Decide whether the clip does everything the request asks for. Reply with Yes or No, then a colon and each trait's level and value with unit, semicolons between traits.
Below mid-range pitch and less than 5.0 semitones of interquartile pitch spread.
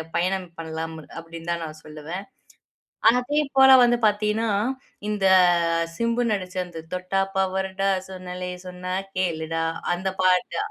No: medium, 185 Hz; average, 3.2 semitones